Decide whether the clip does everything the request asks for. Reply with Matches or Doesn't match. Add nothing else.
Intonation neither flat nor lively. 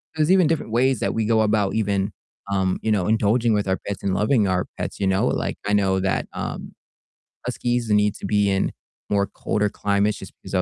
Doesn't match